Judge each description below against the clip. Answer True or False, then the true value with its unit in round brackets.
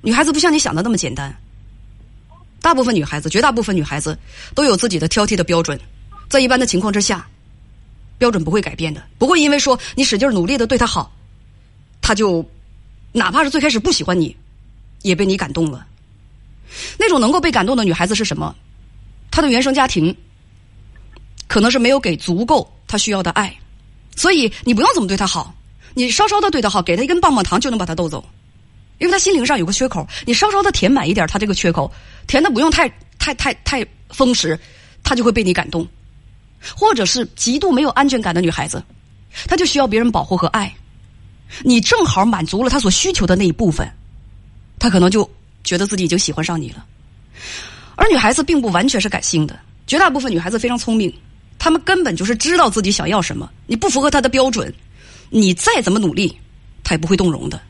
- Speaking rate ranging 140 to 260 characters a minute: False (310 characters per minute)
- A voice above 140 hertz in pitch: True (190 Hz)